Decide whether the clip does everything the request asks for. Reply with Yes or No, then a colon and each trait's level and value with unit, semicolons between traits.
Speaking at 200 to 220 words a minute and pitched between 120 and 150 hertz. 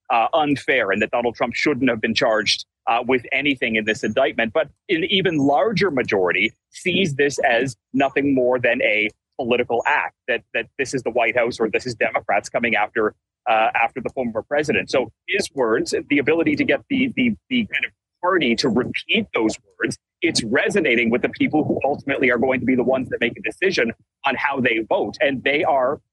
Yes: fast, 205 wpm; medium, 140 Hz